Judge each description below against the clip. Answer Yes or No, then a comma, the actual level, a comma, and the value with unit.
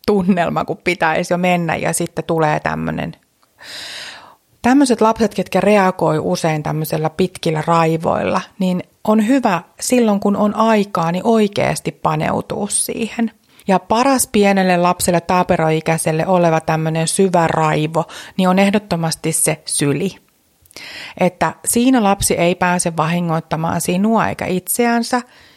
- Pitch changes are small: No, average, 4.4 semitones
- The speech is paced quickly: No, average, 120 wpm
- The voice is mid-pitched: Yes, medium, 180 Hz